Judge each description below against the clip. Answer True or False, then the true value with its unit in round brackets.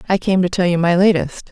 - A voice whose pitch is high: False (180 Hz)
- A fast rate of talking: True (280 wpm)